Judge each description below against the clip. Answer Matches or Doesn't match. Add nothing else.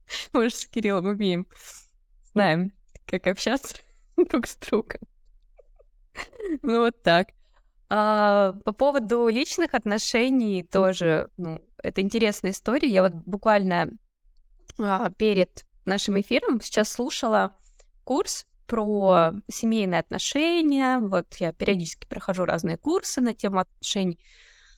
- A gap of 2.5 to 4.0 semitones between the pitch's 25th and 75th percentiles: Doesn't match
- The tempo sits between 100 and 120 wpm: Matches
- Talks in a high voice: Matches